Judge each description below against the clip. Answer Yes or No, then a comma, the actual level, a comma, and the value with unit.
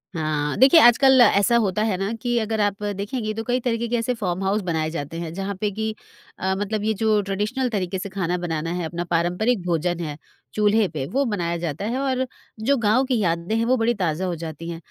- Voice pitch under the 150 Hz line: No, high, 200 Hz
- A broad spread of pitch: No, average, 4.8 semitones